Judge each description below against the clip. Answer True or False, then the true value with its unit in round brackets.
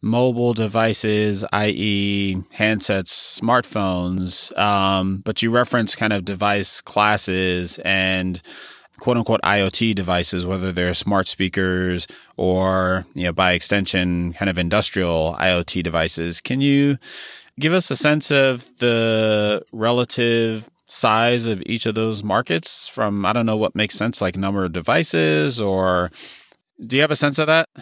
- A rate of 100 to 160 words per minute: True (140 wpm)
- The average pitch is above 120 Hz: False (100 Hz)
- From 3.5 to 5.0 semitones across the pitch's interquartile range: True (3.8 semitones)